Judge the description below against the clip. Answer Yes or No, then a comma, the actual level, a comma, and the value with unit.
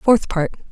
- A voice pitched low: No, high, 200 Hz